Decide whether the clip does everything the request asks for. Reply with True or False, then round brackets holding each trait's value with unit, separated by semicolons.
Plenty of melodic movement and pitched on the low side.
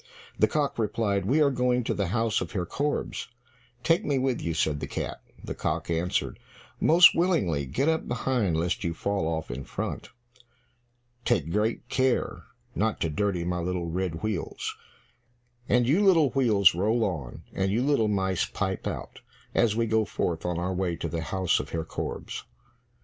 True (6.3 semitones; 100 Hz)